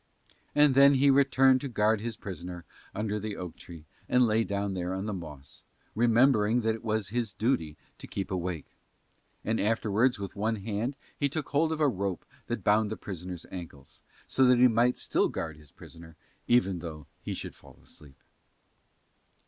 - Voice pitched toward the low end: Yes, low, 105 Hz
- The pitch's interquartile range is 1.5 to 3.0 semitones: No, average, 5.3 semitones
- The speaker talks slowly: No, average, 180 wpm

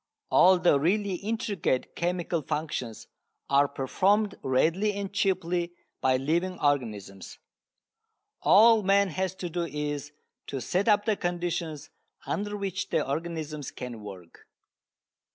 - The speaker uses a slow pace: Yes, slow, 120 wpm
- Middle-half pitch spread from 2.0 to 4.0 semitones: No, wide, 5.4 semitones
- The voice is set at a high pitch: No, medium, 170 Hz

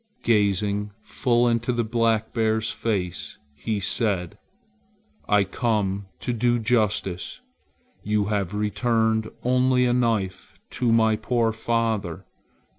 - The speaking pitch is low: Yes, low, 110 Hz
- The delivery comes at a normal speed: No, slow, 115 wpm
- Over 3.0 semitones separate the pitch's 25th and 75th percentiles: No, narrow, 2.4 semitones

